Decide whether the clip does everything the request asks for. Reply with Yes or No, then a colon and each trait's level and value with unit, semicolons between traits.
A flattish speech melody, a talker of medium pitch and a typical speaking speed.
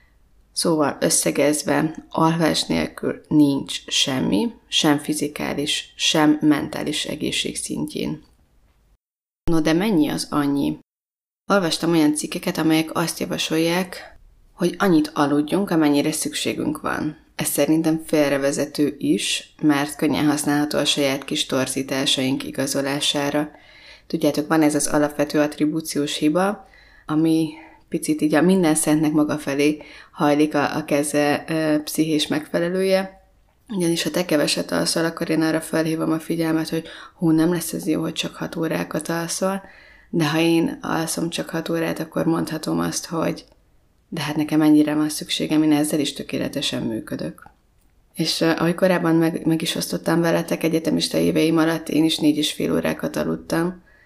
Yes: narrow, 2.0 semitones; medium, 155 Hz; average, 140 wpm